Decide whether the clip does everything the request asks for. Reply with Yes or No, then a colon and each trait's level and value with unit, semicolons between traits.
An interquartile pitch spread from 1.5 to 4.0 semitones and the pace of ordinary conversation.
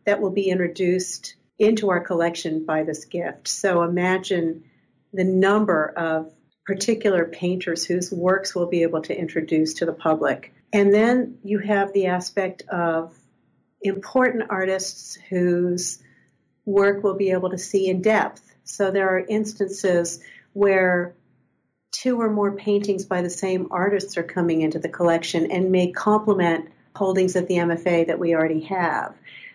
Yes: average, 2.8 semitones; average, 150 wpm